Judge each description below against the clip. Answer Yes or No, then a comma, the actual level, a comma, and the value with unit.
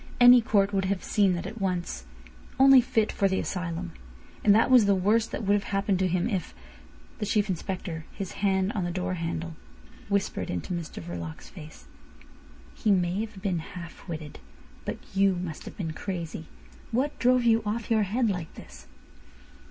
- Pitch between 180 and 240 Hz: Yes, high, 190 Hz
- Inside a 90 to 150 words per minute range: No, average, 175 wpm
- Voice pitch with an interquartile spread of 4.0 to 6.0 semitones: No, average, 3.5 semitones